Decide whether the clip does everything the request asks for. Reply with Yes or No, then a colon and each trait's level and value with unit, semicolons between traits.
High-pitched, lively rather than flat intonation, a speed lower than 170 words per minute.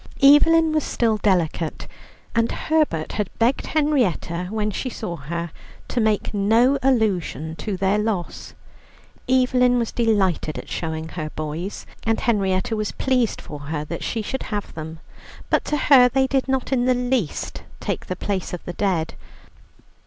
Yes: high, 215 Hz; wide, 6.4 semitones; average, 160 wpm